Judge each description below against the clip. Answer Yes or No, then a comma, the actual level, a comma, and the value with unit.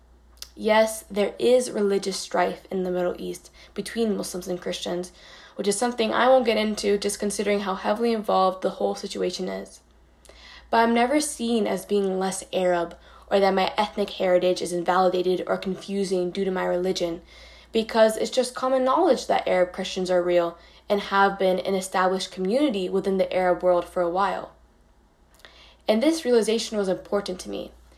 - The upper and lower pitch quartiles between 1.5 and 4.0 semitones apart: Yes, average, 3.0 semitones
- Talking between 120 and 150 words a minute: No, average, 170 wpm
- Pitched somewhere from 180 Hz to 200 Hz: Yes, high, 190 Hz